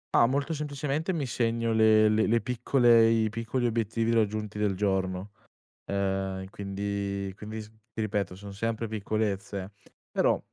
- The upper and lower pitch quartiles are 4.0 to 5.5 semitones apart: No, narrow, 2.5 semitones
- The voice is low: Yes, low, 110 Hz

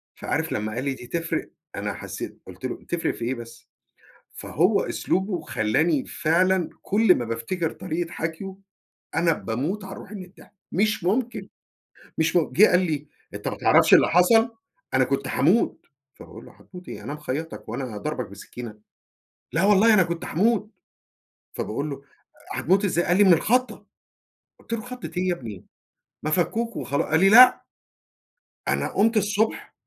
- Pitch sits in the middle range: Yes, medium, 175 Hz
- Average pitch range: No, wide, 6.1 semitones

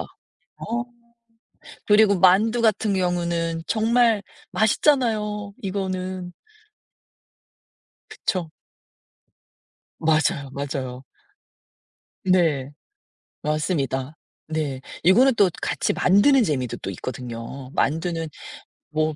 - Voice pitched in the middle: Yes, medium, 175 Hz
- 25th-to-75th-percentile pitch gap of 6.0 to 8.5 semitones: No, wide, 5.6 semitones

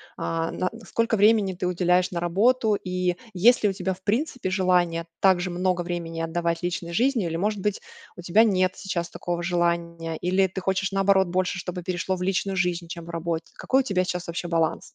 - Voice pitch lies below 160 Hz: No, medium, 180 Hz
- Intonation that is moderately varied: No, narrow, 2.1 semitones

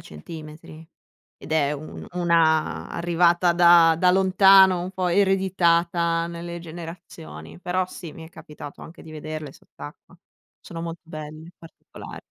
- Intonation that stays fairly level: Yes, narrow, 2.1 semitones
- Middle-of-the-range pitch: Yes, medium, 170 Hz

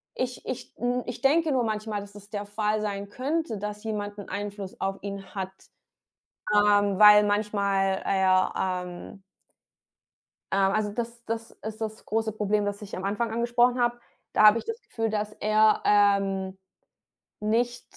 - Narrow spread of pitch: Yes, narrow, 2.1 semitones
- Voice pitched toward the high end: Yes, high, 210 Hz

